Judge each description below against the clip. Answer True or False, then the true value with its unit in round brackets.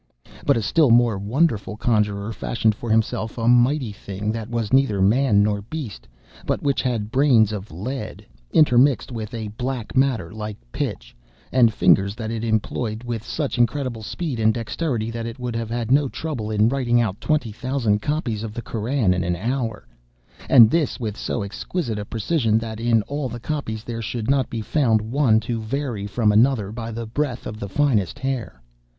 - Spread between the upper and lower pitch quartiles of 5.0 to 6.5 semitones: False (3.3 semitones)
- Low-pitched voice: True (115 Hz)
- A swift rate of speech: False (190 wpm)